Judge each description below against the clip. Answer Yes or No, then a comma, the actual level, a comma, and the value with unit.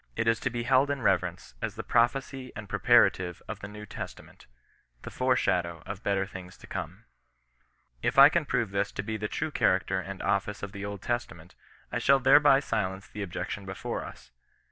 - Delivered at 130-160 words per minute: No, average, 200 wpm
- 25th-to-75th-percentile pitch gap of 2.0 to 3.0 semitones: No, average, 4.5 semitones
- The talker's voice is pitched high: No, low, 105 Hz